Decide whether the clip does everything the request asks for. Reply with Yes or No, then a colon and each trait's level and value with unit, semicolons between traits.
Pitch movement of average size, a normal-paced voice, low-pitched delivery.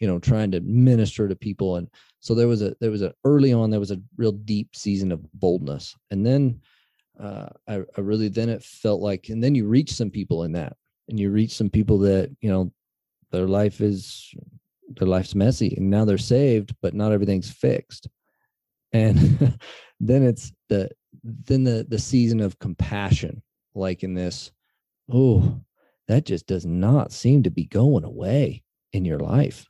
Yes: average, 3.6 semitones; average, 185 wpm; low, 110 Hz